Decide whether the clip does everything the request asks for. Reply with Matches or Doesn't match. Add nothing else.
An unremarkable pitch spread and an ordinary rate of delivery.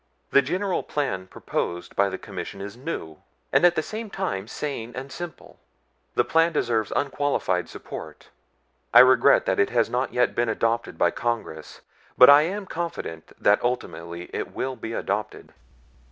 Doesn't match